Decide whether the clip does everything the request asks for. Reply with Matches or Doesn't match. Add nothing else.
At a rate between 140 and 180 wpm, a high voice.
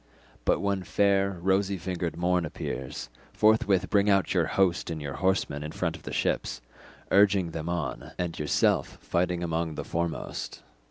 Doesn't match